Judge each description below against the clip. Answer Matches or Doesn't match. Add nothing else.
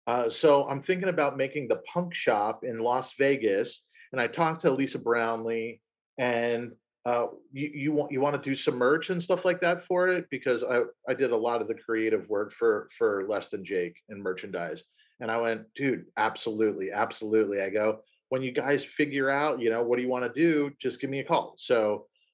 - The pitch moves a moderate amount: Doesn't match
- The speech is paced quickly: Matches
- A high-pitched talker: Doesn't match